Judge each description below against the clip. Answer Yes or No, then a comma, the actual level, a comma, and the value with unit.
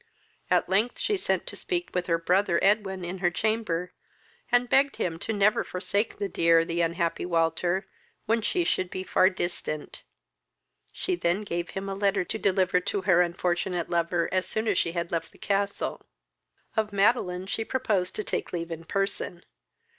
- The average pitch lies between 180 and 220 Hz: Yes, medium, 185 Hz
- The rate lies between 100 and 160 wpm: No, average, 175 wpm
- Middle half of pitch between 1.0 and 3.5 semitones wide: Yes, average, 3.0 semitones